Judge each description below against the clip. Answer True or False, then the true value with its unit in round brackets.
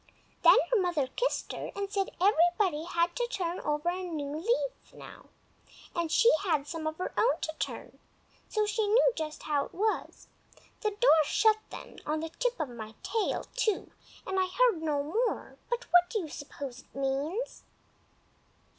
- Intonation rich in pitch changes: True (5.8 semitones)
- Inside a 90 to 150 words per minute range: False (165 wpm)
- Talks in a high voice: True (355 Hz)